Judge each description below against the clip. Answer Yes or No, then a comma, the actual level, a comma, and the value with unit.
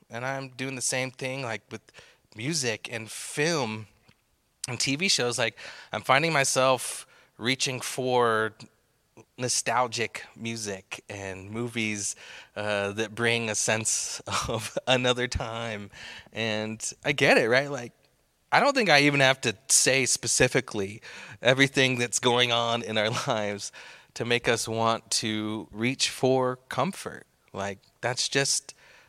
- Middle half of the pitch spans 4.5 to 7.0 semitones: No, average, 3.1 semitones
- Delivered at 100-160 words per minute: Yes, slow, 135 wpm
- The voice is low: Yes, low, 120 Hz